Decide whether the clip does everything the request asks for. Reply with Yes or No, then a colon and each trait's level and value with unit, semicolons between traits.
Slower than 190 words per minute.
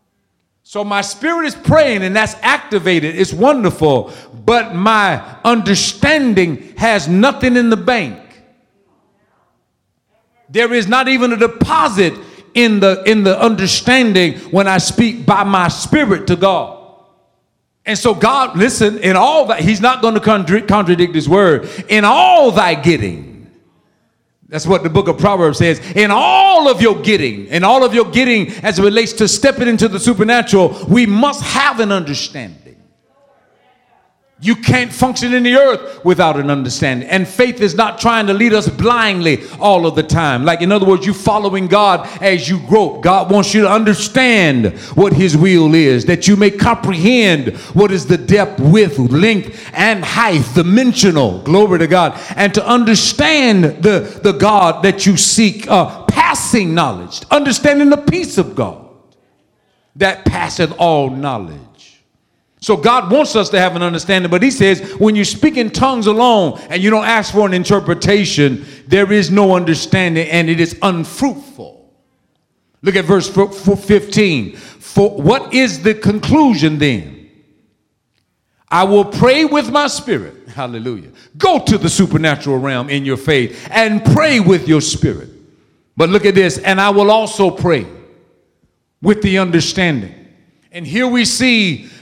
Yes: average, 160 wpm